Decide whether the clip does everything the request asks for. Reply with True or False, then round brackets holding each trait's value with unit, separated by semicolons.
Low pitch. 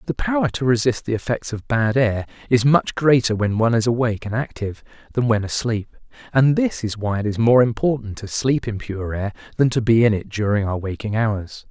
True (115 Hz)